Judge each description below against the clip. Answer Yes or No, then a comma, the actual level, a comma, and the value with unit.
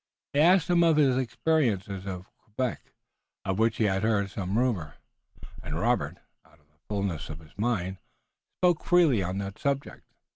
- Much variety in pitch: Yes, wide, 6.5 semitones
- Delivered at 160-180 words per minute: Yes, average, 170 wpm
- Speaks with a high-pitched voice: No, low, 105 Hz